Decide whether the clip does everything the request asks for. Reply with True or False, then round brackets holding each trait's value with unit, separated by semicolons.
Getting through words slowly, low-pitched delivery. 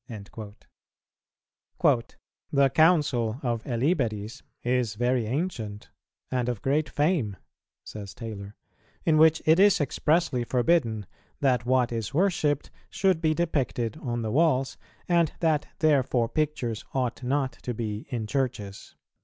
True (125 wpm; 125 Hz)